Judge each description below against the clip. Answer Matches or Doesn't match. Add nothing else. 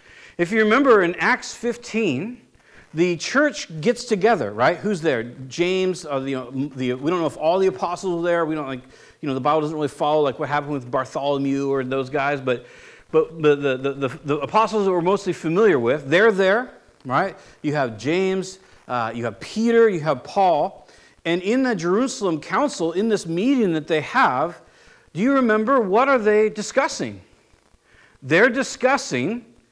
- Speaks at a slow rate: Doesn't match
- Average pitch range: Doesn't match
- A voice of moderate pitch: Matches